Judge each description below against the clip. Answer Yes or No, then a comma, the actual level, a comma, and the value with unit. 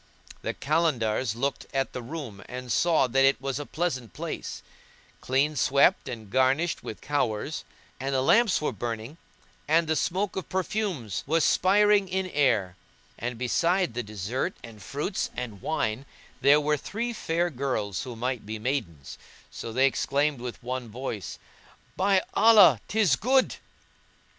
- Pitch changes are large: Yes, wide, 6.0 semitones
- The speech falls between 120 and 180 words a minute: Yes, average, 150 wpm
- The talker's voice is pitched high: No, low, 135 Hz